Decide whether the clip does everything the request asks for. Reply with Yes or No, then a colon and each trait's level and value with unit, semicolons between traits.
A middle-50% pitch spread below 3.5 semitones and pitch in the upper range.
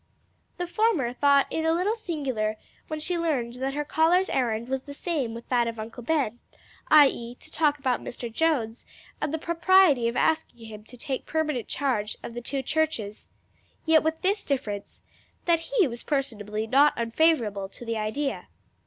No: wide, 5.4 semitones; very high, 275 Hz